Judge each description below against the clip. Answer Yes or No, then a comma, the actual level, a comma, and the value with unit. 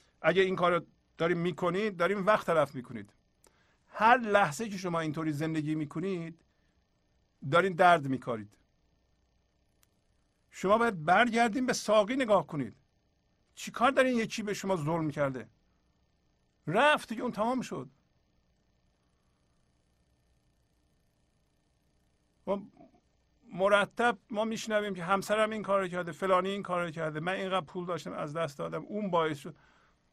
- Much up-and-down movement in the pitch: Yes, wide, 8.3 semitones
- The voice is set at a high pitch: No, medium, 175 Hz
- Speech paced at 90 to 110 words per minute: No, average, 125 wpm